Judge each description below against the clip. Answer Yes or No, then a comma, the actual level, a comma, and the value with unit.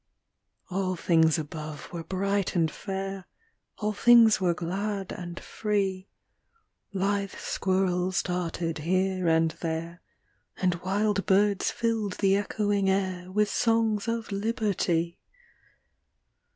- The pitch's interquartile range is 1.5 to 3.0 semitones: Yes, average, 2.7 semitones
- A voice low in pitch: No, high, 190 Hz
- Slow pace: Yes, slow, 110 wpm